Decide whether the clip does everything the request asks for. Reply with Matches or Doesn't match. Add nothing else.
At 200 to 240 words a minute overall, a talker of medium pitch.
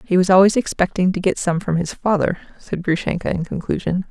Matches